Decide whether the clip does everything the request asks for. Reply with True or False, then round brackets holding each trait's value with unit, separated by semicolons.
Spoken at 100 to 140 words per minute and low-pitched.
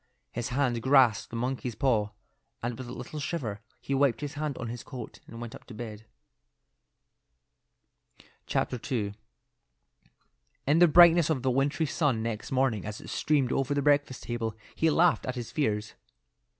False (165 wpm; 130 Hz)